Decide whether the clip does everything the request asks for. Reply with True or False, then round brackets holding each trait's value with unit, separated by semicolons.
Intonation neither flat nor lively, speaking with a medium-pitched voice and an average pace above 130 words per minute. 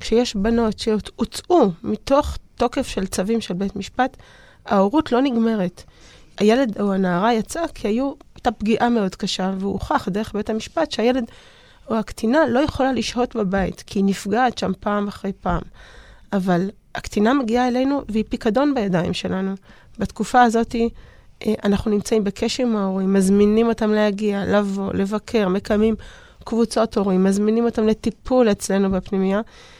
False (3.1 semitones; 220 Hz; 140 wpm)